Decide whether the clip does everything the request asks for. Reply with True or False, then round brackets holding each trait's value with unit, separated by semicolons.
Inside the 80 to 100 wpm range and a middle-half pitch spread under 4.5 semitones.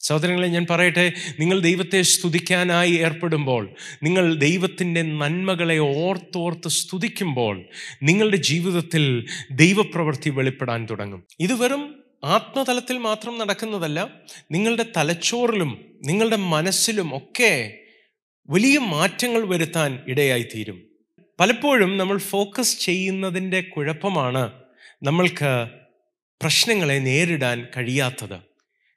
False (85 wpm; 5.2 semitones)